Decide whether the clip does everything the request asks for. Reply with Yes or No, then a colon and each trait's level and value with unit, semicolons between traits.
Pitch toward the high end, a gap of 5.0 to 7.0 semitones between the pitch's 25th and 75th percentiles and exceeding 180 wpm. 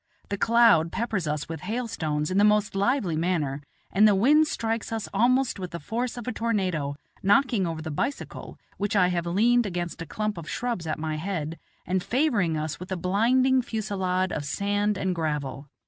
Yes: high, 195 Hz; wide, 5.5 semitones; average, 190 wpm